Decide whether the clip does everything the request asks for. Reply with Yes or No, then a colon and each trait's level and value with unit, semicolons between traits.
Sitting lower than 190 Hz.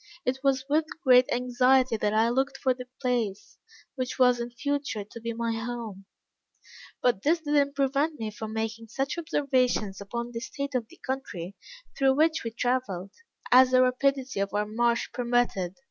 No: very high, 250 Hz